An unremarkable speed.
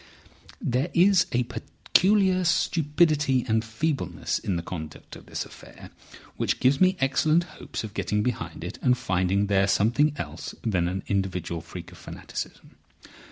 Yes: average, 150 wpm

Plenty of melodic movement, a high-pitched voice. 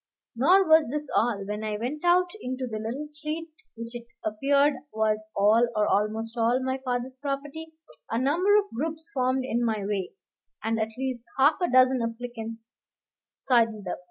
No: average, 4.6 semitones; very high, 250 Hz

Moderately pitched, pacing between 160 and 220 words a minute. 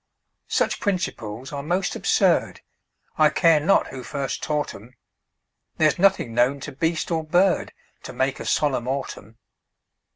No: medium, 145 Hz; average, 140 wpm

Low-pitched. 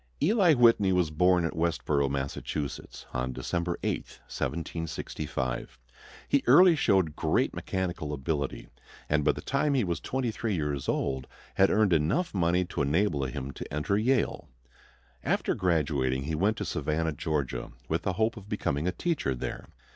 Yes: very low, 85 Hz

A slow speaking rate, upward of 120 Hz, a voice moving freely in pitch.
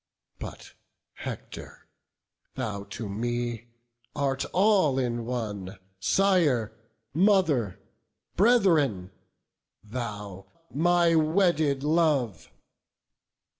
Yes: slow, 70 wpm; low, 135 Hz; wide, 7.3 semitones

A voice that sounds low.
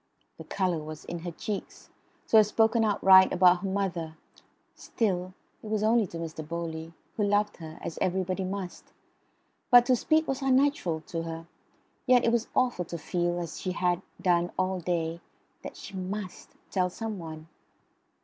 No: medium, 185 Hz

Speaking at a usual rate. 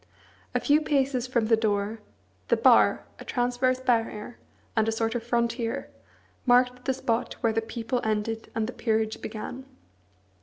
Yes: average, 155 wpm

